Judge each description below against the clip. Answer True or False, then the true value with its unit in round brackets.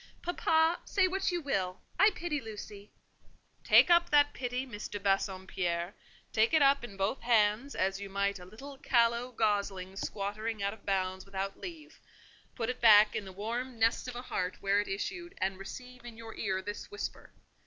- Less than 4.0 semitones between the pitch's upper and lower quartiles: False (5.0 semitones)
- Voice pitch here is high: True (220 Hz)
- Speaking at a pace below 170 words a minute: False (185 wpm)